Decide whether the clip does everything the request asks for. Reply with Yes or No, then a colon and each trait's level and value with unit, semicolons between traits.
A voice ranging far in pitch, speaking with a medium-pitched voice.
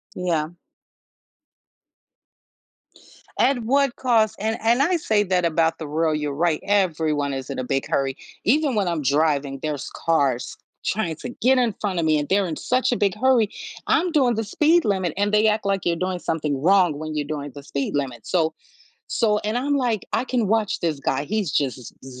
Yes: wide, 6.7 semitones; medium, 180 Hz